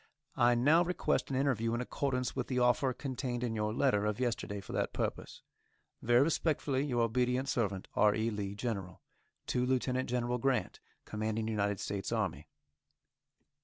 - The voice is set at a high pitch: No, low, 120 Hz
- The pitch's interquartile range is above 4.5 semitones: No, average, 3.1 semitones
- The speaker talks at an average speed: Yes, average, 160 wpm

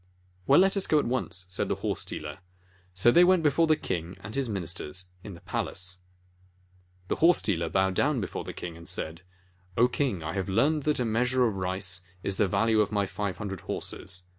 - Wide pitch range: Yes, wide, 5.9 semitones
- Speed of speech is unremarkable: No, fast, 210 wpm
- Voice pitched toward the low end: Yes, low, 100 Hz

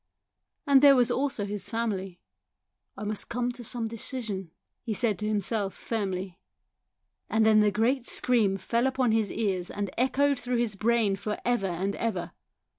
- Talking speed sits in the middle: Yes, average, 170 wpm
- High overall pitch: Yes, high, 220 Hz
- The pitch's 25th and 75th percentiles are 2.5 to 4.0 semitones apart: Yes, average, 3.4 semitones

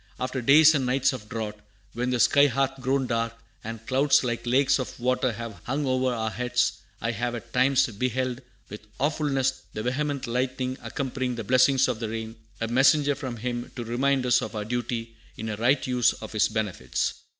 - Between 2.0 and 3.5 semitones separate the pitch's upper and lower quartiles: Yes, narrow, 2.6 semitones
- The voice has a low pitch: Yes, low, 125 Hz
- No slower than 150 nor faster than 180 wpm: No, average, 195 wpm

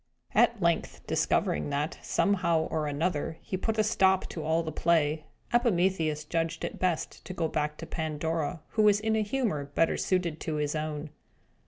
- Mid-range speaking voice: Yes, medium, 165 Hz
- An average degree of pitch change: Yes, average, 3.6 semitones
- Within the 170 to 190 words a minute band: Yes, average, 175 wpm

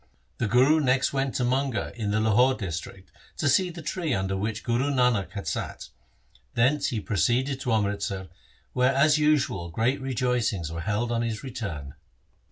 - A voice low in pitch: Yes, low, 120 Hz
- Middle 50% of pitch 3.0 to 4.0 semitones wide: No, average, 4.7 semitones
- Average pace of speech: Yes, average, 170 wpm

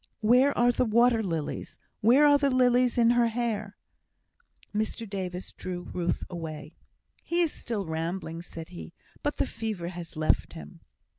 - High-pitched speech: Yes, high, 210 Hz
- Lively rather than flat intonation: Yes, wide, 5.9 semitones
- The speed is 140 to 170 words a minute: Yes, average, 155 wpm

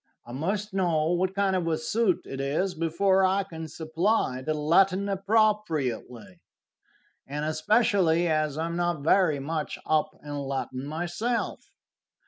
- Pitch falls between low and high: Yes, medium, 165 Hz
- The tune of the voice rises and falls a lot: No, average, 4.0 semitones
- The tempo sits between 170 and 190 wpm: No, average, 140 wpm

